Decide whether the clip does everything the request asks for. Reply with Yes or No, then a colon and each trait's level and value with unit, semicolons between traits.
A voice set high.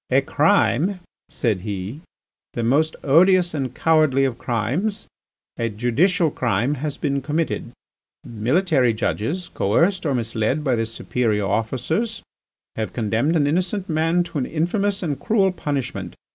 No: medium, 140 Hz